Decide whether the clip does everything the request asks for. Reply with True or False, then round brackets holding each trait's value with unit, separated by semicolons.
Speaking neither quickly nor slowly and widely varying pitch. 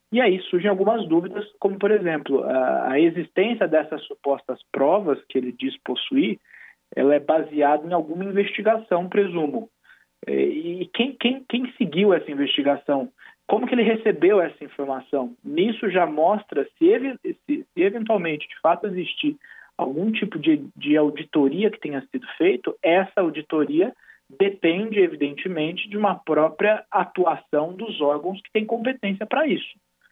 True (145 wpm; 6.5 semitones)